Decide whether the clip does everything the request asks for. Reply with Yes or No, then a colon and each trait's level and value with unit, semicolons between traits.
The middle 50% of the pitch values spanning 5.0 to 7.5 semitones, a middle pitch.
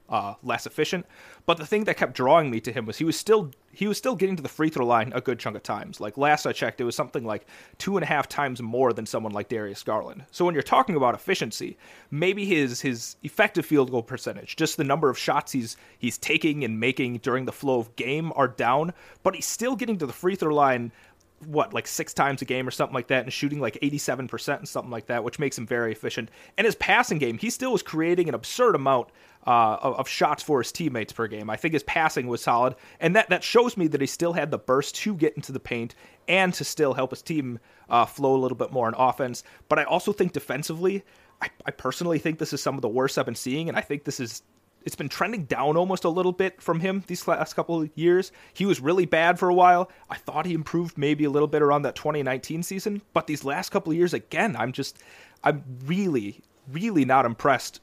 Yes: average, 5.3 semitones; medium, 150 Hz